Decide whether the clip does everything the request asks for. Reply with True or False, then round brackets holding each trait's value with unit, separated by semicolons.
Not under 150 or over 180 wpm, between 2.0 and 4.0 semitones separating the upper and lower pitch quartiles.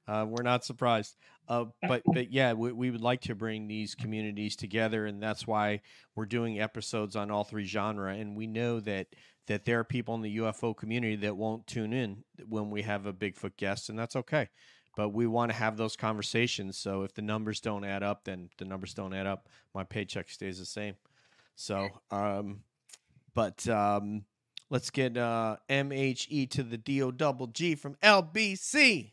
False (190 wpm; 2.9 semitones)